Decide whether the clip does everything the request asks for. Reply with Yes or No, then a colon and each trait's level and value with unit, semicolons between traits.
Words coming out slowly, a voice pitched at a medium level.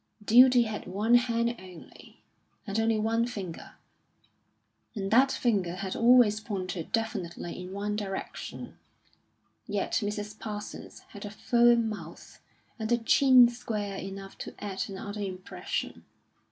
No: slow, 125 wpm; high, 210 Hz